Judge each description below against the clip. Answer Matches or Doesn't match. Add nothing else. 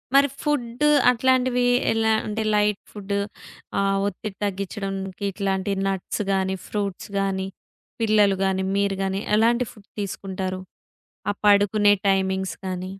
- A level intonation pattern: Matches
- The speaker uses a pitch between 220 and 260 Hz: Doesn't match